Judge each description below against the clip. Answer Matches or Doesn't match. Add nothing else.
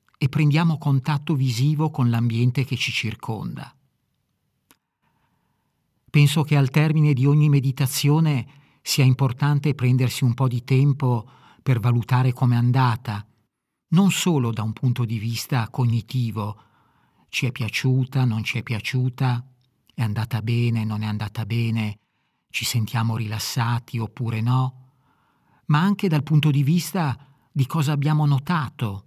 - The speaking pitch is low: Matches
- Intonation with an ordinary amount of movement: Matches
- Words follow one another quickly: Doesn't match